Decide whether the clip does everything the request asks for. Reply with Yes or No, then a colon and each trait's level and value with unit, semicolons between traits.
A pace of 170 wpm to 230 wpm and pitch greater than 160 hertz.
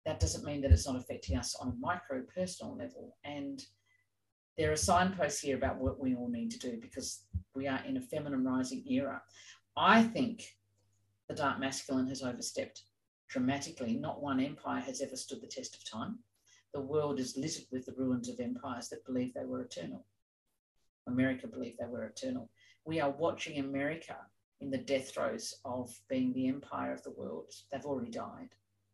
No: average, 180 wpm; medium, 140 Hz